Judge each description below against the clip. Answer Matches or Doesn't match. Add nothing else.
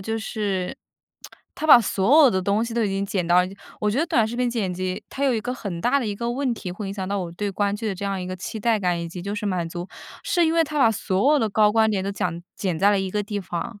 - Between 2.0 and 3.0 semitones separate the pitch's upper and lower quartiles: Doesn't match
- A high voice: Matches